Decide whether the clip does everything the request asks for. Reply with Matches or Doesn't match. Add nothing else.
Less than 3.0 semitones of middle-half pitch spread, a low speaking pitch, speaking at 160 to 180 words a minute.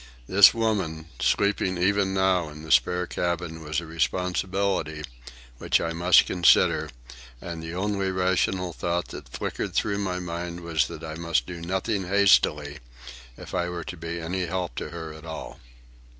Matches